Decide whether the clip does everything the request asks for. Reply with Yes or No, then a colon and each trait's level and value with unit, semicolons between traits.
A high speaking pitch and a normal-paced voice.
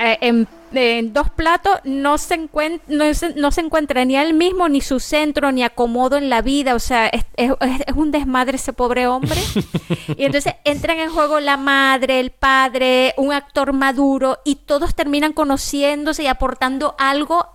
Yes: very high, 275 Hz; average, 180 wpm